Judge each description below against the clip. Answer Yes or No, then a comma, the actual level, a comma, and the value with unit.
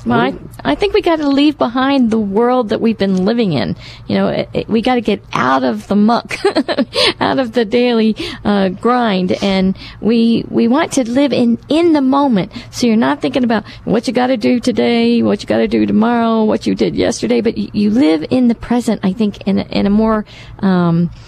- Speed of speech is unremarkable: No, fast, 225 wpm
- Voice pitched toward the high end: Yes, high, 225 Hz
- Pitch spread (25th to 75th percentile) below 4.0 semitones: No, average, 4.3 semitones